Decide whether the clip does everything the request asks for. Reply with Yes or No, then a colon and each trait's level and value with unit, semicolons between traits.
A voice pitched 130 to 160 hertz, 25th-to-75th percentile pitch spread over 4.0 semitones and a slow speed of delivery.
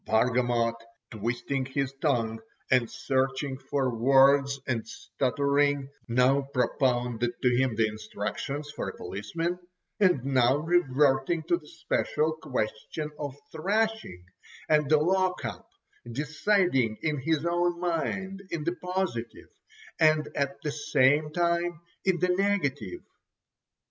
Yes: medium, 140 Hz; average, 5.0 semitones; slow, 120 wpm